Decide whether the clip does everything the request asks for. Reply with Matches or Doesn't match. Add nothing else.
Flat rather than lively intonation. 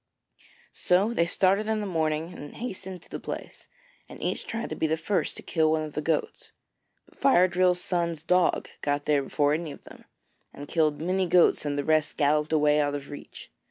Doesn't match